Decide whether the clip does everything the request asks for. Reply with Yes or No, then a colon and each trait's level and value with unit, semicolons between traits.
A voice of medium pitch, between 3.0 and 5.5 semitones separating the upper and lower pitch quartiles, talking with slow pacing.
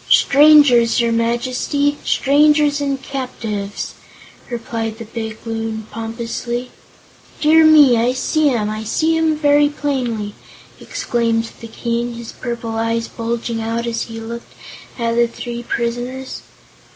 No: high, 235 Hz; average, 3.3 semitones; slow, 125 wpm